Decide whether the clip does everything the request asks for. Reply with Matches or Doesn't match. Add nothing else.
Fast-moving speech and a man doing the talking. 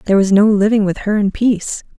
Doesn't match